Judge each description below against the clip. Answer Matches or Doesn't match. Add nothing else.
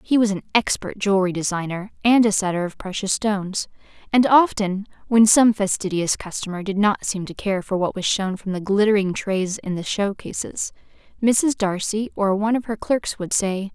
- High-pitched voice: Matches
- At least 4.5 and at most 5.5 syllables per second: Matches